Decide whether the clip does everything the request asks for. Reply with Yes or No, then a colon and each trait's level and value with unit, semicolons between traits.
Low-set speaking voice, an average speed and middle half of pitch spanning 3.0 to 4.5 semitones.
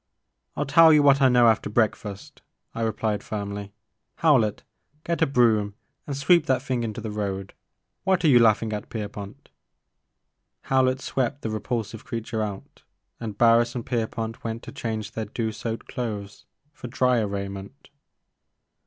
Yes: low, 115 Hz; average, 160 wpm; average, 3.4 semitones